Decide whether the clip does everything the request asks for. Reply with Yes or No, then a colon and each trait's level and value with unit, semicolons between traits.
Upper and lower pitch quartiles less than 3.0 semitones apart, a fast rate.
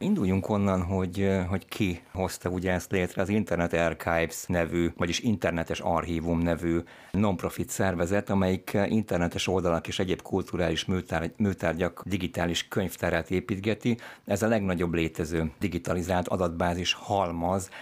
No: narrow, 2.6 semitones; average, 120 wpm